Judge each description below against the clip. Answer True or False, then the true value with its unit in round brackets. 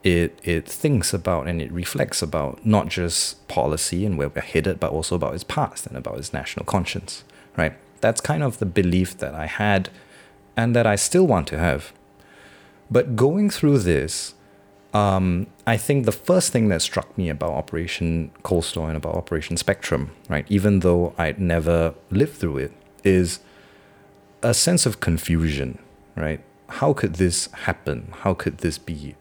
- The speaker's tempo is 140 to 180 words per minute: True (170 wpm)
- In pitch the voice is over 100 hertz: False (95 Hz)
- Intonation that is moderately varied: True (3.6 semitones)